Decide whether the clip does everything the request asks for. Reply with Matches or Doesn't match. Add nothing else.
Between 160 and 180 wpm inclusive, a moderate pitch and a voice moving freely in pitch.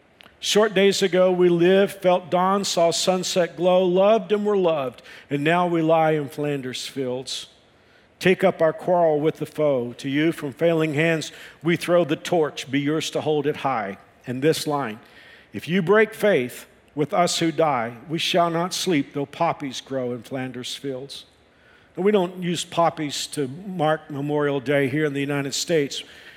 Doesn't match